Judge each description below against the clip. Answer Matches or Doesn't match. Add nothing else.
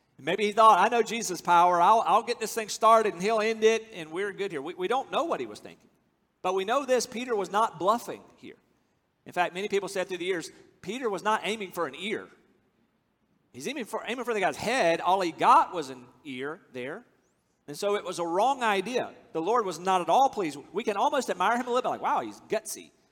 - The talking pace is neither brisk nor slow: Doesn't match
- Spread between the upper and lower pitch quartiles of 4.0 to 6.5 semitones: Matches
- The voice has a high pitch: Matches